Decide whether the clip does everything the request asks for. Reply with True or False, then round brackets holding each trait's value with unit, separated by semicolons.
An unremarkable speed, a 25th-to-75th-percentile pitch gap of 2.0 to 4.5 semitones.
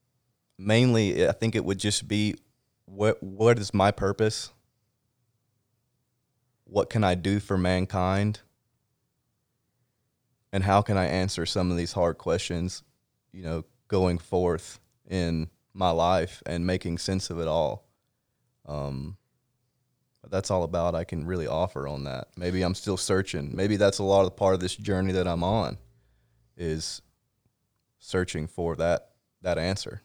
False (150 wpm; 4.9 semitones)